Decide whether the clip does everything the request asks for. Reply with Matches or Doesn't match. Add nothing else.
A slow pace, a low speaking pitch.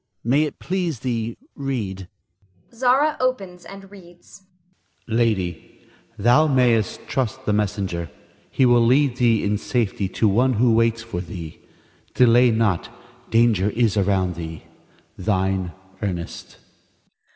Matches